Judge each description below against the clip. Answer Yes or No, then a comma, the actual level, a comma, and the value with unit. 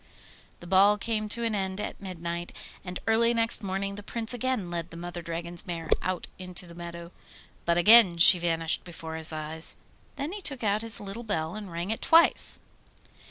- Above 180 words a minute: Yes, average, 190 wpm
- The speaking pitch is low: No, medium, 185 Hz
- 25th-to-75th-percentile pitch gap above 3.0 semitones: Yes, average, 4.1 semitones